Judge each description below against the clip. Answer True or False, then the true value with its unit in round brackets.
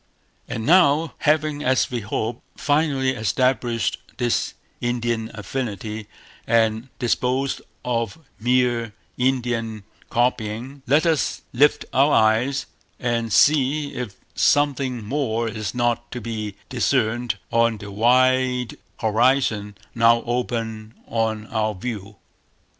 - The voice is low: True (120 Hz)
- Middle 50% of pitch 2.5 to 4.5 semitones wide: True (2.9 semitones)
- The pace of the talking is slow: True (110 wpm)